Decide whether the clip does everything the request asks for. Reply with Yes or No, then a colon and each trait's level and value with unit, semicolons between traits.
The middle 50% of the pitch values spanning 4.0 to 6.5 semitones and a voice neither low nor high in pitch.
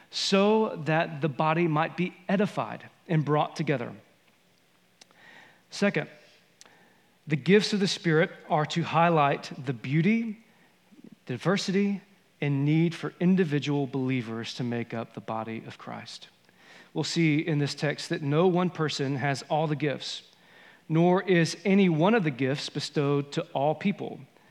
Yes: average, 4.7 semitones; medium, 160 Hz